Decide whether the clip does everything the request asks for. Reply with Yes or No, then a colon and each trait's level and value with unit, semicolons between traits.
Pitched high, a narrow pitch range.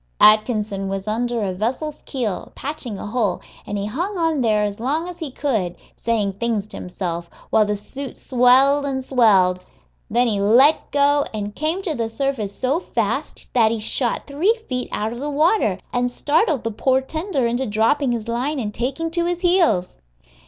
No: high, 245 Hz; wide, 5.4 semitones